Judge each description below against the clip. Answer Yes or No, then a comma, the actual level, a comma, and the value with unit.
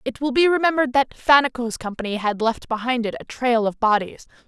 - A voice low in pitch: No, high, 245 Hz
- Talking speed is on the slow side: No, average, 200 wpm